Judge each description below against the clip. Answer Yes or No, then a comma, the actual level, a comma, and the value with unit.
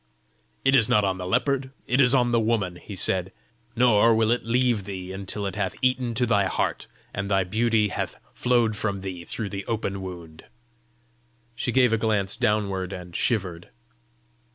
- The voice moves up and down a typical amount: Yes, average, 3.8 semitones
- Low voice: Yes, low, 105 Hz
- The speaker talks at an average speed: Yes, average, 175 wpm